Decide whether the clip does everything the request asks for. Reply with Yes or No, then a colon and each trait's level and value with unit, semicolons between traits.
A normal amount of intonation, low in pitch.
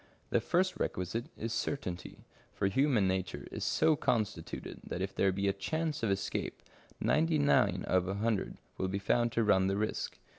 Yes: average, 4.3 semitones; low, 100 Hz